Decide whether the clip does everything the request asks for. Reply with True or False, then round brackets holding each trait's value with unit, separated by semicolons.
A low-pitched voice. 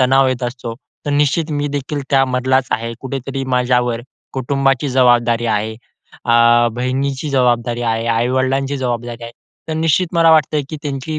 True (130 Hz)